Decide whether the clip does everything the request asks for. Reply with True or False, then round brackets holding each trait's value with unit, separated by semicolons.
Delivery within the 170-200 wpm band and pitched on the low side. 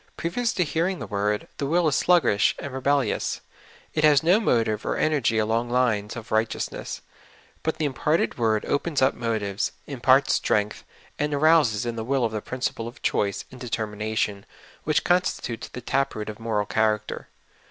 True (175 wpm; 120 Hz)